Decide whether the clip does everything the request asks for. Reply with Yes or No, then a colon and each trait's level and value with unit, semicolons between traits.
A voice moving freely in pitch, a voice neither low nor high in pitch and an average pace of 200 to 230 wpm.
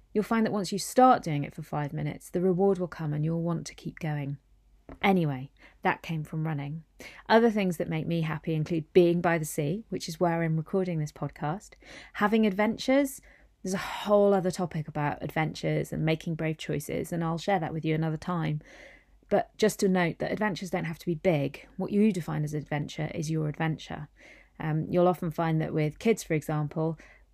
No: average, 3.4 semitones; medium, 165 Hz; fast, 205 wpm